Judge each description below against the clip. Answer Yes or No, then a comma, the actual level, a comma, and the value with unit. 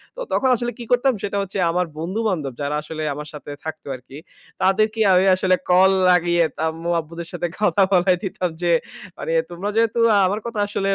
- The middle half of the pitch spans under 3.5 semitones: No, average, 3.8 semitones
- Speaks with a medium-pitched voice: Yes, medium, 180 Hz